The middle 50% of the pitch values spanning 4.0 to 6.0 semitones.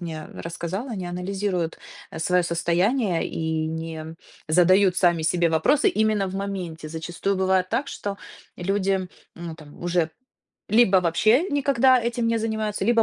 Yes: average, 4.3 semitones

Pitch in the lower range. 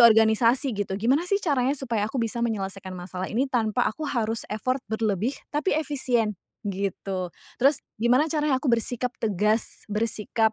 No: high, 230 Hz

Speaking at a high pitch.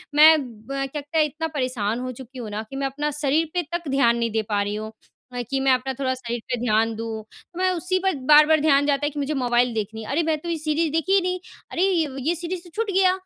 Yes: very high, 280 Hz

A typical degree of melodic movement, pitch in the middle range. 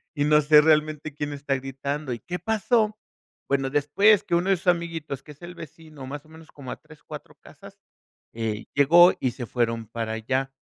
Yes: average, 3.8 semitones; medium, 145 Hz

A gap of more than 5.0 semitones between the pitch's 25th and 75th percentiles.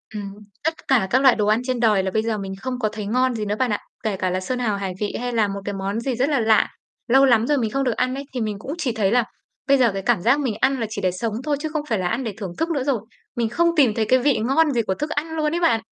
No: average, 4.3 semitones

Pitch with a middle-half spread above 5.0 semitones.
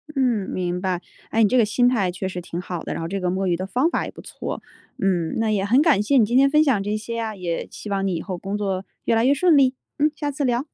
Yes: wide, 5.4 semitones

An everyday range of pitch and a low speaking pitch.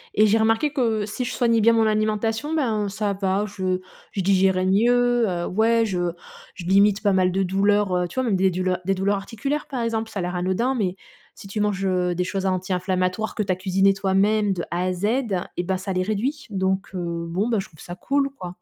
No: average, 3.0 semitones; high, 195 Hz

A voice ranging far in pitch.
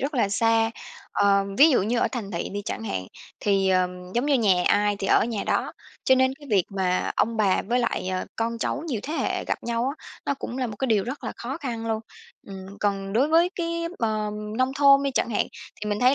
No: average, 4.7 semitones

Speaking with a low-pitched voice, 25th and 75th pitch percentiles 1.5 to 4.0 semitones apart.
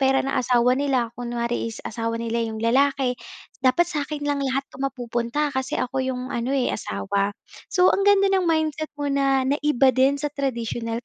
No: very high, 265 Hz; average, 3.1 semitones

